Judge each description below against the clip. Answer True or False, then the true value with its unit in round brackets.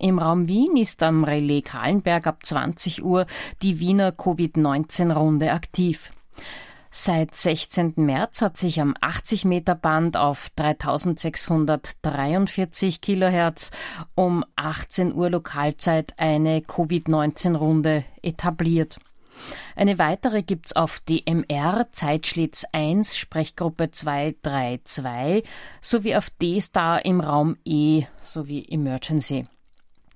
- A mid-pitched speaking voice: True (165 Hz)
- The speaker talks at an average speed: False (100 wpm)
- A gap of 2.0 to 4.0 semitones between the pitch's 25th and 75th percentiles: True (2.9 semitones)